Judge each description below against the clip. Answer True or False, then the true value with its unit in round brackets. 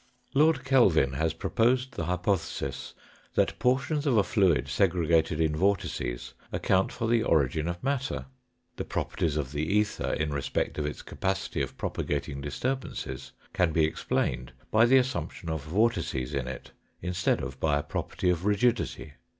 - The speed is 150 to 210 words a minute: True (160 wpm)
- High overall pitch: False (90 Hz)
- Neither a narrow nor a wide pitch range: False (7.3 semitones)